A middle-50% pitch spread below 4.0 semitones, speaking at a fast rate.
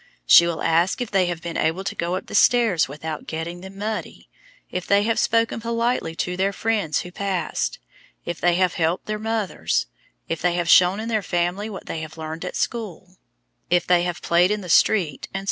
Yes: average, 3.6 semitones; fast, 210 wpm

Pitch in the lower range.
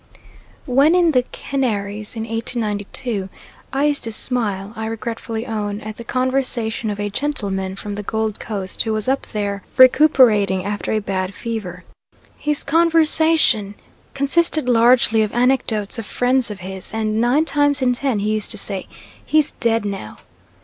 No: high, 225 Hz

